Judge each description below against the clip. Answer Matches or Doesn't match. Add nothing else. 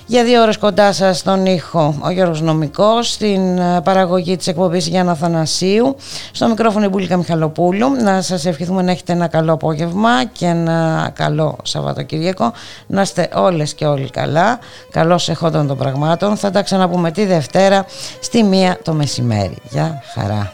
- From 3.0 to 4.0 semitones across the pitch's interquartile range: Matches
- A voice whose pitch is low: Doesn't match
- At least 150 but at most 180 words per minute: Matches